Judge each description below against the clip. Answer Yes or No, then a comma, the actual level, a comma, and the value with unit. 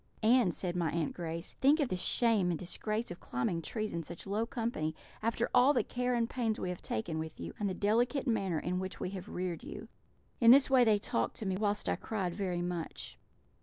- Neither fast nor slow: No, fast, 225 wpm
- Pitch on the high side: Yes, high, 200 Hz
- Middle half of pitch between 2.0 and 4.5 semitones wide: No, average, 4.9 semitones